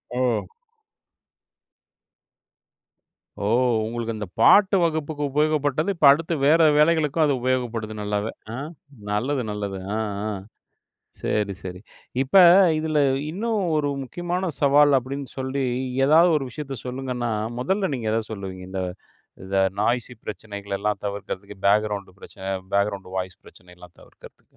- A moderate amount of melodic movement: No, wide, 6.6 semitones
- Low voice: Yes, low, 125 Hz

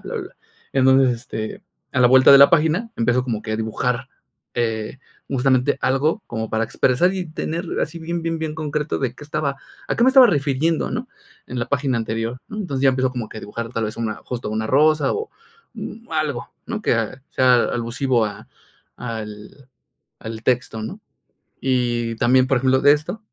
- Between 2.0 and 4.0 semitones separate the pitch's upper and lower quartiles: No, average, 4.7 semitones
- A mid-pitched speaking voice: No, low, 130 Hz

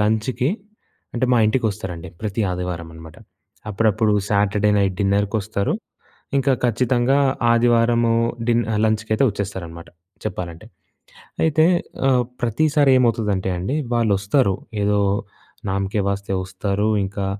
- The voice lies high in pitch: No, low, 105 Hz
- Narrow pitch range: No, average, 3.4 semitones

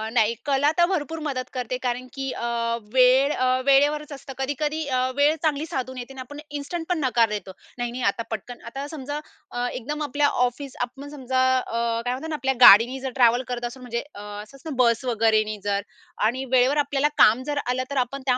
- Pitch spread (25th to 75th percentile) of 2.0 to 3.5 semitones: Yes, average, 2.9 semitones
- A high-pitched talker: Yes, very high, 260 Hz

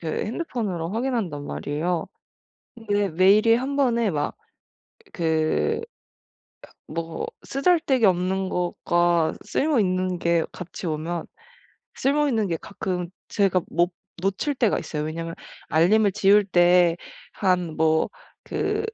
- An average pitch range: Yes, average, 4.7 semitones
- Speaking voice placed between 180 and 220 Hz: Yes, medium, 185 Hz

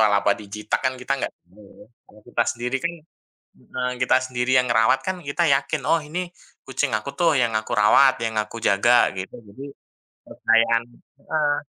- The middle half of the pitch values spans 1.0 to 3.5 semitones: No, average, 4.1 semitones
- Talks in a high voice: No, low, 125 Hz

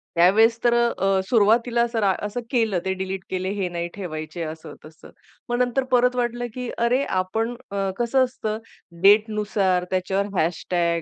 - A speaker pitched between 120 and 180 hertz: No, high, 210 Hz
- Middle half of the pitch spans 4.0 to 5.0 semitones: Yes, average, 4.3 semitones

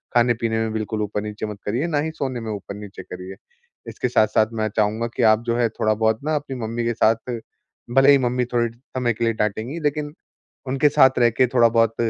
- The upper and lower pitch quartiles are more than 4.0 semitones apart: No, average, 3.0 semitones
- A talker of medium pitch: No, low, 115 Hz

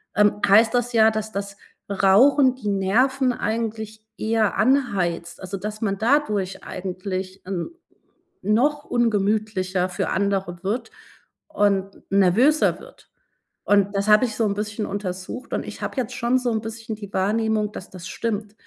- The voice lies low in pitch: No, high, 210 Hz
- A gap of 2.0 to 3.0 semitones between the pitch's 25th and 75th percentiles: Yes, average, 2.7 semitones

